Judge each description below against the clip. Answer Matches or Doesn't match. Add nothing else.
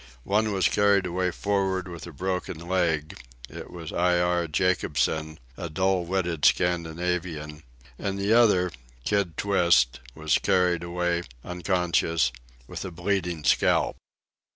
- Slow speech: Matches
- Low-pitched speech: Matches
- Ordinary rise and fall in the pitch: Doesn't match